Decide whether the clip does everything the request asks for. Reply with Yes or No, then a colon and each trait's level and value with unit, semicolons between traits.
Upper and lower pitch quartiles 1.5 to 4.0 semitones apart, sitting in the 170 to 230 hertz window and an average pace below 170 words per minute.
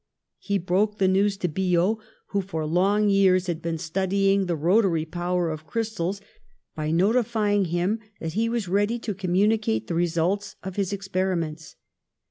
Yes: average, 3.1 semitones; high, 190 Hz; average, 160 wpm